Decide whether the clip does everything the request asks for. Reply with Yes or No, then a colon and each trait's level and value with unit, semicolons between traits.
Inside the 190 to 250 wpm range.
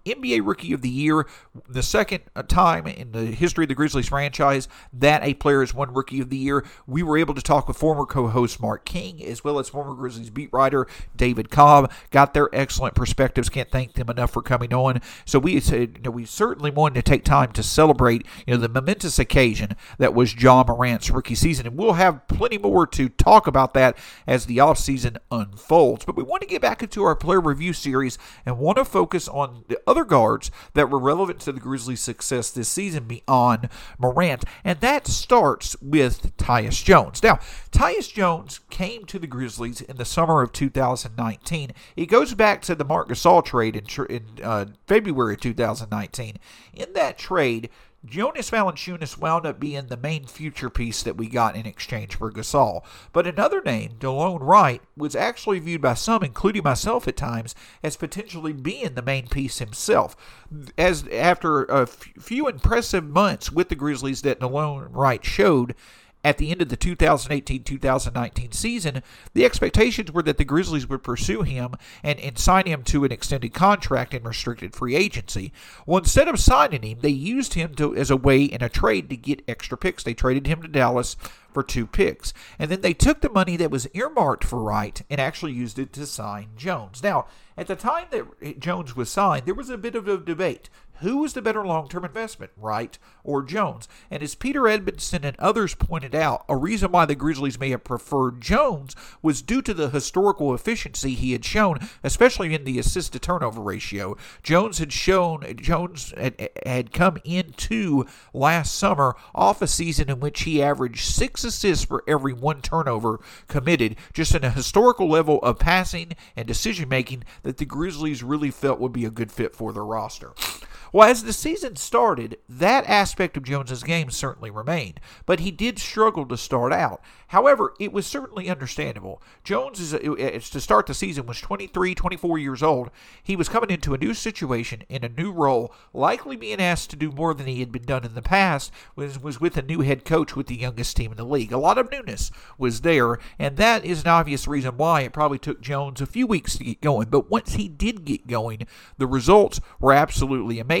Yes: average, 195 wpm